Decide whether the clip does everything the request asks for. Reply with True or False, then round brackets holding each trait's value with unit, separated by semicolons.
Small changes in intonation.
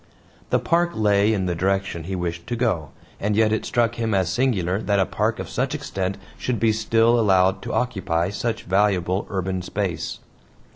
False (3.4 semitones)